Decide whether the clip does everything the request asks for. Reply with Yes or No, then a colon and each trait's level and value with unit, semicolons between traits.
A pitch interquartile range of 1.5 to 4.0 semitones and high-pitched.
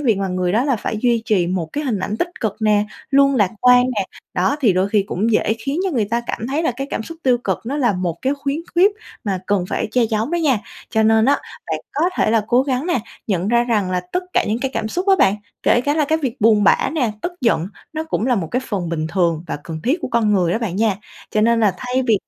No: average, 5.1 semitones; high, 225 Hz